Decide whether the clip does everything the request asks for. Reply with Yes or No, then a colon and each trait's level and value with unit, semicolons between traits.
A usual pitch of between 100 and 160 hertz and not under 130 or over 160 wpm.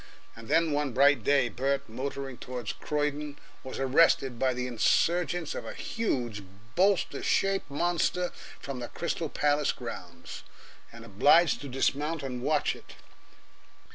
Yes: medium, 140 Hz; average, 140 wpm